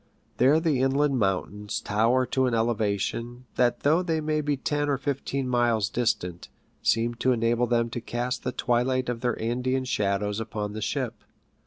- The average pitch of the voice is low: Yes, low, 120 Hz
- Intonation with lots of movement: No, average, 2.8 semitones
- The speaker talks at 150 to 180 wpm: Yes, average, 170 wpm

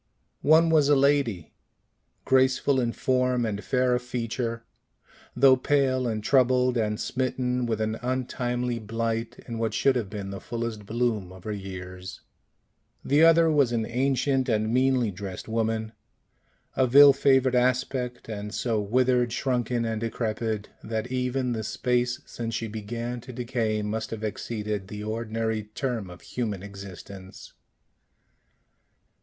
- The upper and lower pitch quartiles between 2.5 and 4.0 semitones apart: Yes, average, 2.9 semitones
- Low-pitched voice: Yes, low, 120 Hz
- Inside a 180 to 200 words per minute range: No, average, 140 wpm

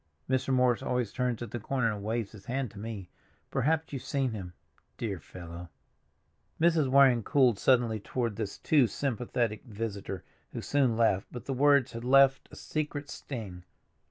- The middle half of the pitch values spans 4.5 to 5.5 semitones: No, average, 4.1 semitones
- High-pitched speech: No, low, 120 Hz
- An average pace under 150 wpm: No, average, 160 wpm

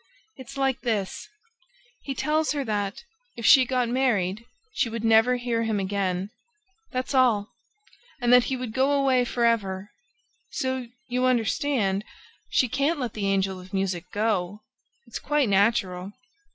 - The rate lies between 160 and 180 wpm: No, average, 150 wpm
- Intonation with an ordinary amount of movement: Yes, average, 4.5 semitones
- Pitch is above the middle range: Yes, high, 230 Hz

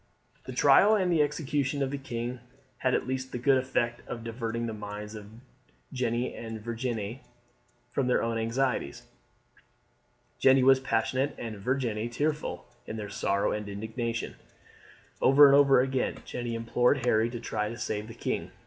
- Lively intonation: No, average, 2.8 semitones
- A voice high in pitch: No, low, 120 Hz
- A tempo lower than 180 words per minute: Yes, average, 160 wpm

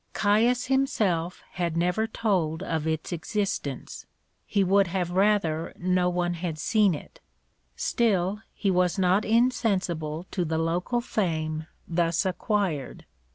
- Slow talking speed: Yes, slow, 125 wpm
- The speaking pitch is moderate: Yes, medium, 180 Hz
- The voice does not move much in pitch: No, average, 3.8 semitones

